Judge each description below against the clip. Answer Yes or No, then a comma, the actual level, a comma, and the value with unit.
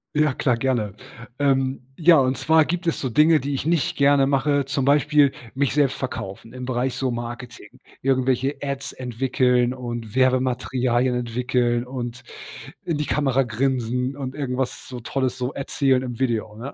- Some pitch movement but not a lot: No, narrow, 2.1 semitones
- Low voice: Yes, low, 130 Hz